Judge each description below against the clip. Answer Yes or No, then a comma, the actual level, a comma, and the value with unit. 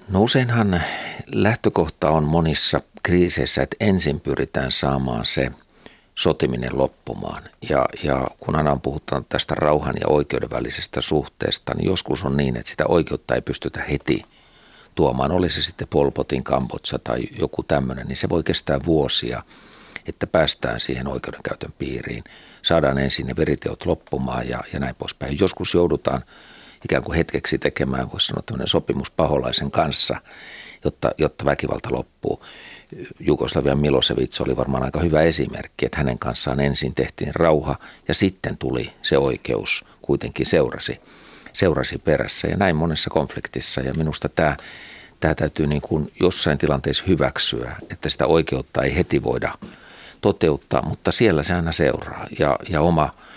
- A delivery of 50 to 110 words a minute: No, average, 145 wpm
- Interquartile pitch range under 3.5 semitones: No, average, 3.9 semitones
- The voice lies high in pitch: No, very low, 70 Hz